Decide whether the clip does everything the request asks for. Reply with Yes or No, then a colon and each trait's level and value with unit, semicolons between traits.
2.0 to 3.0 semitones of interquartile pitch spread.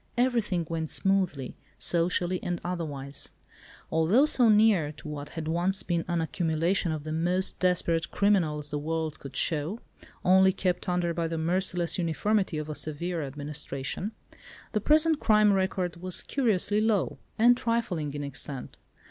No: average, 3.8 semitones